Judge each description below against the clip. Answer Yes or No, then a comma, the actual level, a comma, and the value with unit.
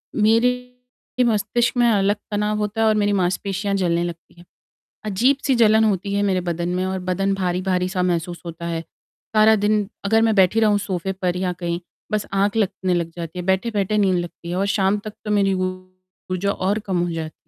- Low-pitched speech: No, high, 195 Hz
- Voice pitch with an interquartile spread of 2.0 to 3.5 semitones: Yes, average, 2.8 semitones